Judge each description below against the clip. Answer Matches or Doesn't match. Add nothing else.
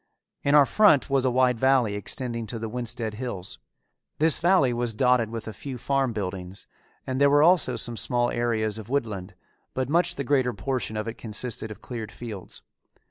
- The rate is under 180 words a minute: Doesn't match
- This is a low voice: Matches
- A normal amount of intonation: Matches